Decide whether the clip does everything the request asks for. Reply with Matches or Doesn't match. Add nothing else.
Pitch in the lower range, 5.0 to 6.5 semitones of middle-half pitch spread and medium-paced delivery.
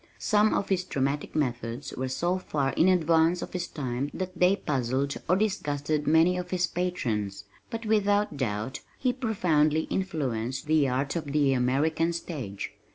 Doesn't match